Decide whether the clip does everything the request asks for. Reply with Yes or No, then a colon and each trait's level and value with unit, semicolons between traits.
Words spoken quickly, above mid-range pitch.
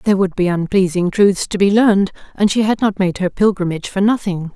Yes: fast, 225 wpm; high, 195 Hz